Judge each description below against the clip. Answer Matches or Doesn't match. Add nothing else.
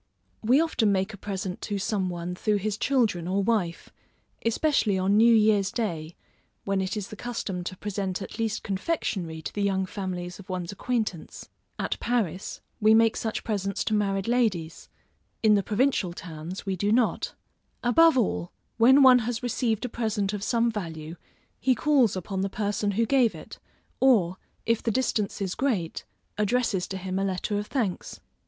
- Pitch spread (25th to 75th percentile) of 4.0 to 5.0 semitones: Doesn't match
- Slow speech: Doesn't match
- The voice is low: Doesn't match